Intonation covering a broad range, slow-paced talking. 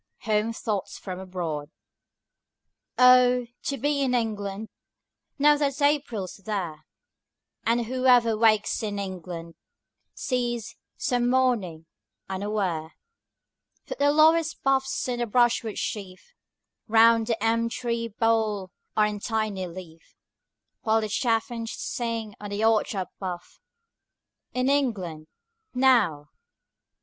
No: average, 4.2 semitones; slow, 115 wpm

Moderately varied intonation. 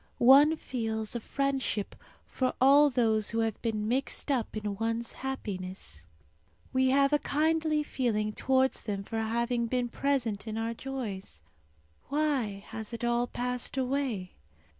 Yes: average, 3.6 semitones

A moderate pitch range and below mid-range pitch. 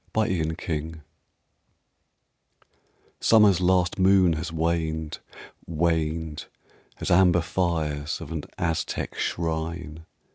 No: narrow, 1.9 semitones; very low, 80 Hz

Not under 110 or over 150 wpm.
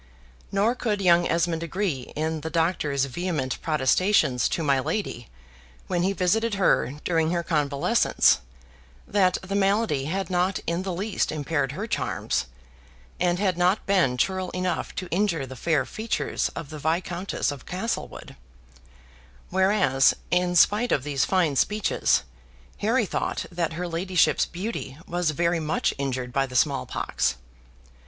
Yes: average, 145 wpm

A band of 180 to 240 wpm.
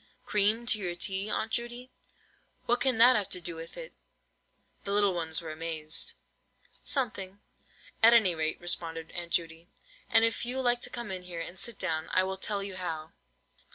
Yes: average, 185 wpm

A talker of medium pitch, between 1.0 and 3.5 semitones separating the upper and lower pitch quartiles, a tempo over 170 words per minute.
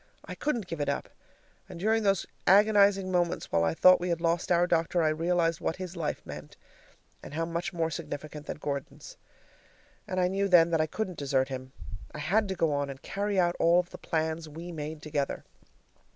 Yes: medium, 170 Hz; average, 3.2 semitones; fast, 205 wpm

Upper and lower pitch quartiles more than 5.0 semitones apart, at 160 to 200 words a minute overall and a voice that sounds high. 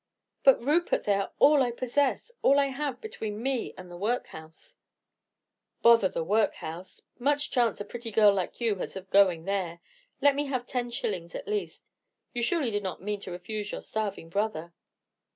Yes: wide, 5.5 semitones; average, 180 wpm; high, 220 Hz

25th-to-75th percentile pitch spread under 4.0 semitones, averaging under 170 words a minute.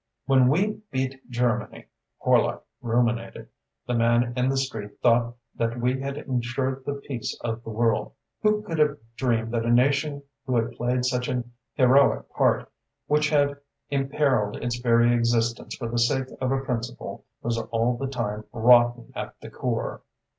Yes: narrow, 2.4 semitones; average, 160 wpm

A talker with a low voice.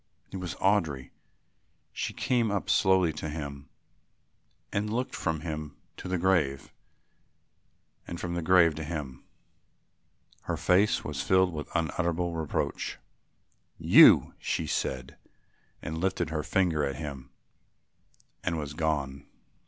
Yes: very low, 80 Hz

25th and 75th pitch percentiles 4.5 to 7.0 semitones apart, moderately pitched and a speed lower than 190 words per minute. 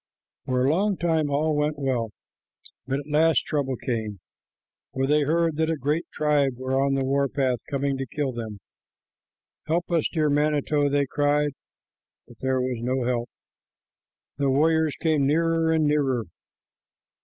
No: average, 2.7 semitones; medium, 145 Hz; average, 155 wpm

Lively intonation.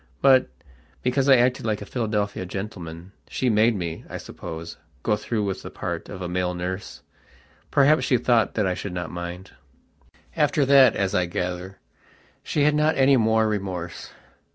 Yes: wide, 5.8 semitones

